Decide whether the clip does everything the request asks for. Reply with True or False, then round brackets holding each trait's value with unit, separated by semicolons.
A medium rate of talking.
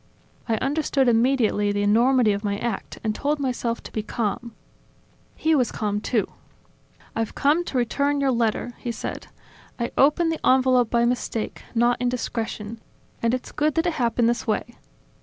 True (165 wpm)